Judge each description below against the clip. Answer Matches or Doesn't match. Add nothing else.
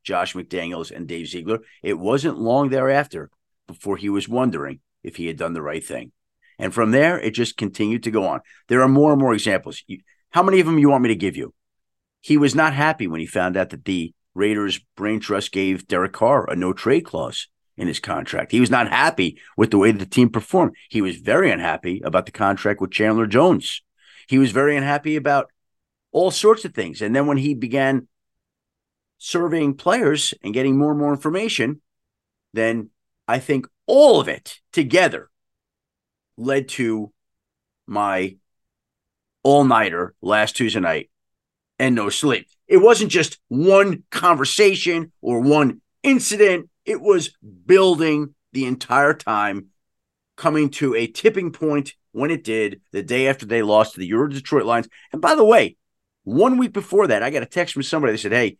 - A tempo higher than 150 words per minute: Matches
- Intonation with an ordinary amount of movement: Doesn't match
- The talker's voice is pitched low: Matches